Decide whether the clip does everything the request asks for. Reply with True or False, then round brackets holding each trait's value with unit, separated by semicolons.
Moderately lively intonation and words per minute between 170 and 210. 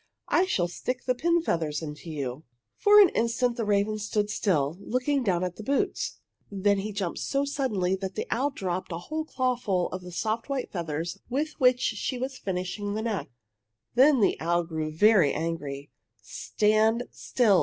False (6.3 semitones; 175 wpm)